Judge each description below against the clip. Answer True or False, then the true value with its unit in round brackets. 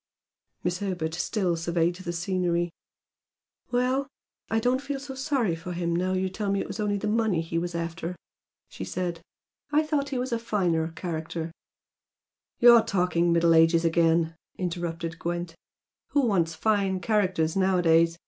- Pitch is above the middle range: False (180 Hz)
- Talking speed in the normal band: True (160 wpm)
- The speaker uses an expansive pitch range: False (4.1 semitones)